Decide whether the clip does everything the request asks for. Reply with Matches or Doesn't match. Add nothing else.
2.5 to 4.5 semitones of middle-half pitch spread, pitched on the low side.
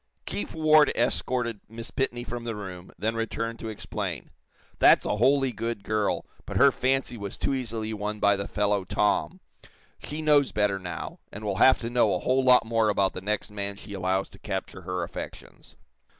Matches